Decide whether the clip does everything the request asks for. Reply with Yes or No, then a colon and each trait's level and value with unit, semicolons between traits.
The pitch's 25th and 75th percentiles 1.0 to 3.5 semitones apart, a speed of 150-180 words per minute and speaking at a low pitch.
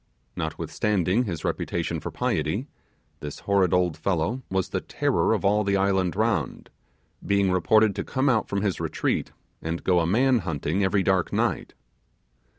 Yes: average, 3.2 semitones; average, 155 wpm; very low, 95 Hz